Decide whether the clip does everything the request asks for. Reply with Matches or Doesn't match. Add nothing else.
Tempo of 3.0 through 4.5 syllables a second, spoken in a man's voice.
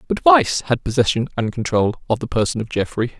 Doesn't match